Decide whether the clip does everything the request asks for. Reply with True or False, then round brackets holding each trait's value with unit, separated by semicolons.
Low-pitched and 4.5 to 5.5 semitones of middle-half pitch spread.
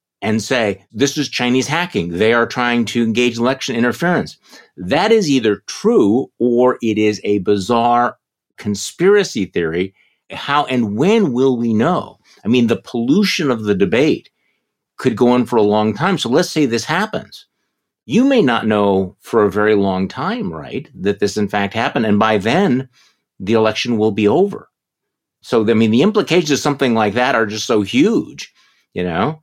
True (120 Hz; 4.8 semitones)